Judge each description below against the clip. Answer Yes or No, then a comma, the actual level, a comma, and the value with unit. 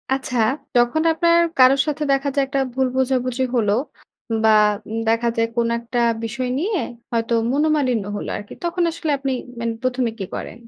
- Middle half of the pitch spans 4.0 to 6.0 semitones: No, average, 3.2 semitones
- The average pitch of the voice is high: Yes, very high, 255 Hz